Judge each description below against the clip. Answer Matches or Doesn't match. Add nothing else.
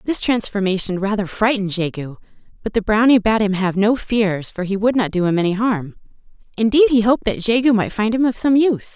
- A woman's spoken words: Matches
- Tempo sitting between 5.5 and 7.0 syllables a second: Matches